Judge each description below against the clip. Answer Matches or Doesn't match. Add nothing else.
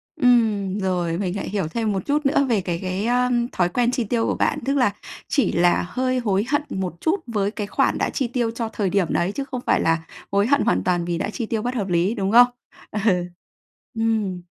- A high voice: Matches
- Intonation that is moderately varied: Matches